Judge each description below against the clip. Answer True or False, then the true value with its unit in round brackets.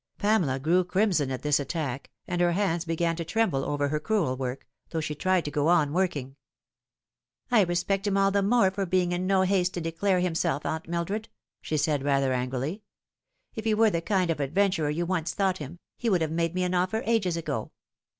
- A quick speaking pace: True (215 wpm)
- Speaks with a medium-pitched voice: True (175 Hz)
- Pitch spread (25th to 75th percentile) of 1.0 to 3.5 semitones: False (4.2 semitones)